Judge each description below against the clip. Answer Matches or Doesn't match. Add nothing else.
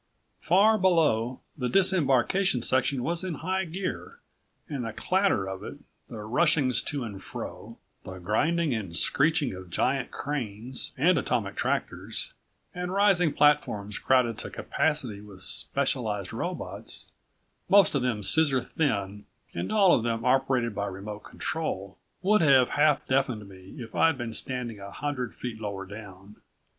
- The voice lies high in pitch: Doesn't match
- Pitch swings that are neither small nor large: Doesn't match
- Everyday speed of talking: Matches